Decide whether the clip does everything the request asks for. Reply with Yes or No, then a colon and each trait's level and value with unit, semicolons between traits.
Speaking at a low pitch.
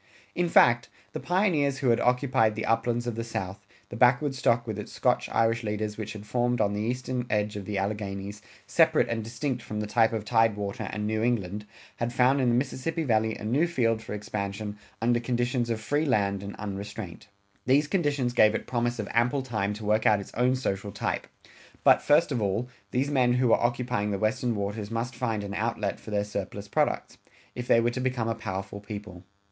Yes: low, 115 Hz